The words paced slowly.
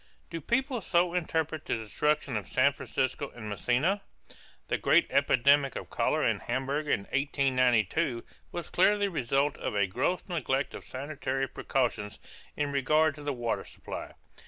No: average, 155 wpm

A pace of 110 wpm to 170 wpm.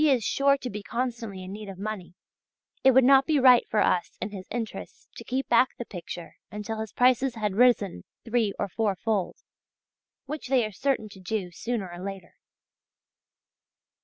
No: average, 180 wpm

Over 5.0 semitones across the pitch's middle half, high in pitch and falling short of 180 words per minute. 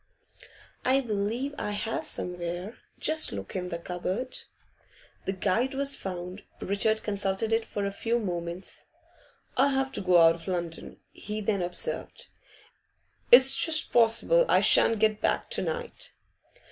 Yes: wide, 5.5 semitones; high, 210 Hz; average, 145 wpm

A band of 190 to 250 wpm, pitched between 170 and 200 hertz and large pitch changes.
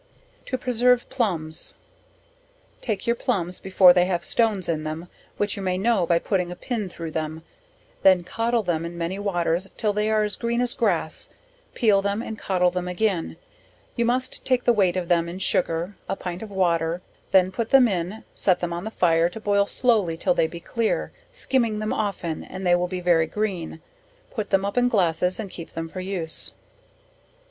No: average, 195 wpm; high, 190 Hz; average, 4.0 semitones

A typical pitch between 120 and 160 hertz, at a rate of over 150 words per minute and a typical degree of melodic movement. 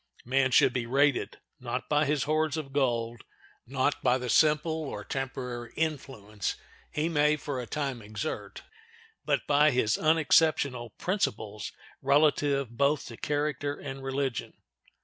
No: medium, 140 Hz; slow, 135 wpm; average, 3.3 semitones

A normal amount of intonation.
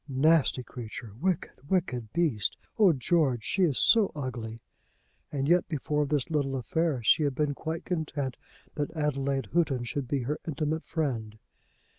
Yes: average, 3.9 semitones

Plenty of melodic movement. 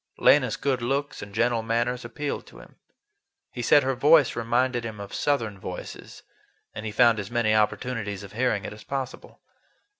No: average, 3.1 semitones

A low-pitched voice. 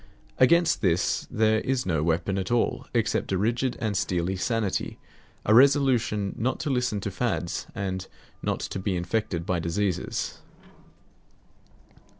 Yes: low, 100 Hz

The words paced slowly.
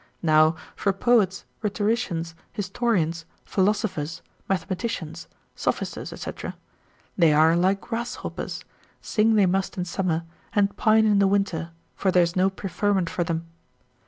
Yes: slow, 130 wpm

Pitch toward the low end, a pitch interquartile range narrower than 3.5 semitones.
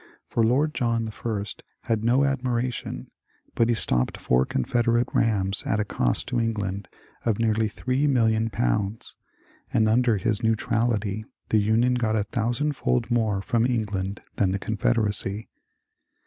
Yes: low, 110 Hz; narrow, 2.6 semitones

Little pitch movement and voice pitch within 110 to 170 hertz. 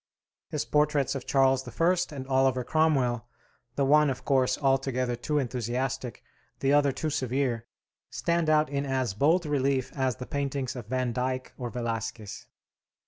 Yes: narrow, 2.3 semitones; low, 135 Hz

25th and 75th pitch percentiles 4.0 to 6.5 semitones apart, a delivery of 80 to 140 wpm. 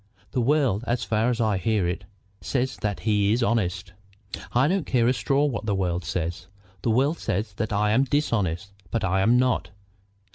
No: average, 4.4 semitones; average, 190 wpm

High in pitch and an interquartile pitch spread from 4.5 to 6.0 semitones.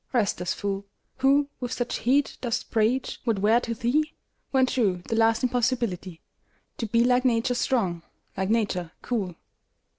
No: high, 230 Hz; average, 3.9 semitones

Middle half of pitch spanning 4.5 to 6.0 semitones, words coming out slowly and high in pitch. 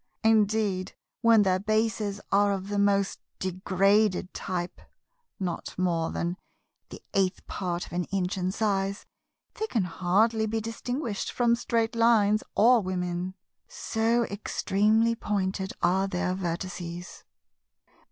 No: average, 3.1 semitones; slow, 125 wpm; high, 200 Hz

